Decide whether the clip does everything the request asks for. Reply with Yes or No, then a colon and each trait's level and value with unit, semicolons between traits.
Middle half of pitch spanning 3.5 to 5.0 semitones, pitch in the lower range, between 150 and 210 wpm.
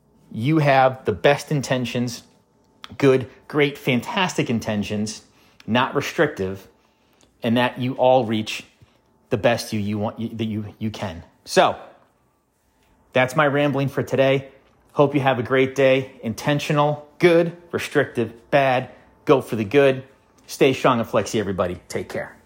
No: average, 4.0 semitones; low, 130 Hz; average, 140 wpm